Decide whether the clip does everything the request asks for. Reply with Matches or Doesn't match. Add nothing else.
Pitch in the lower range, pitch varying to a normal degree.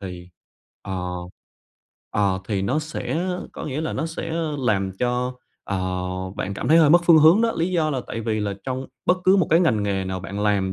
Doesn't match